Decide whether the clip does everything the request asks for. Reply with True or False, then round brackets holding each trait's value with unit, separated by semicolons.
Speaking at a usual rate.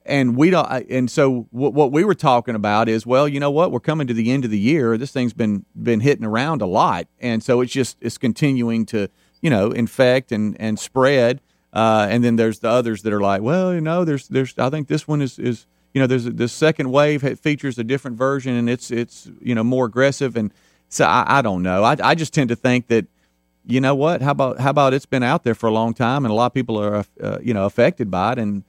False (255 wpm)